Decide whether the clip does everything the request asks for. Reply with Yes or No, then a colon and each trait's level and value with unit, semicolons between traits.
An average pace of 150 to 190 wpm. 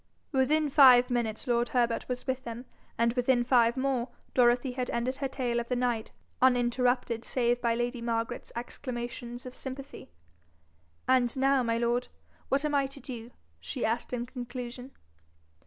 Yes: average, 155 wpm